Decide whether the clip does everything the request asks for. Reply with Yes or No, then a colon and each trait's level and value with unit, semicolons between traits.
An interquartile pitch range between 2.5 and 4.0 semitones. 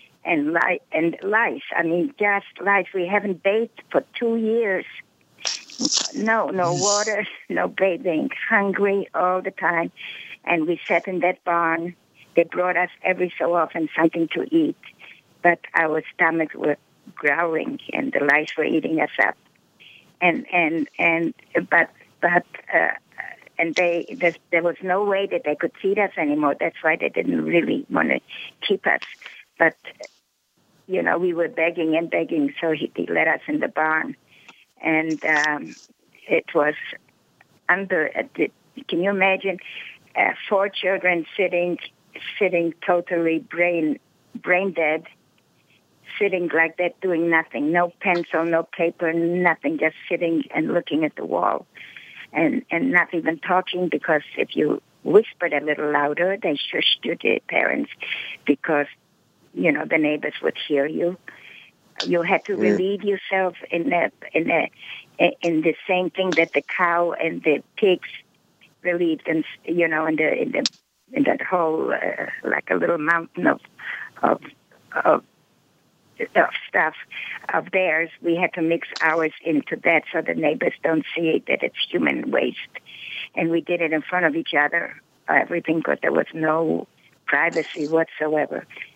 Yes: average, 2.8 semitones